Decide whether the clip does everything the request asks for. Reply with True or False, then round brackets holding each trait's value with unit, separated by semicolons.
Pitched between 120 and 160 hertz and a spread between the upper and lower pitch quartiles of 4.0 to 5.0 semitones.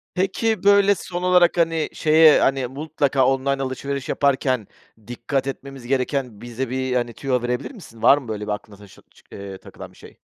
True (135 Hz; 4.3 semitones)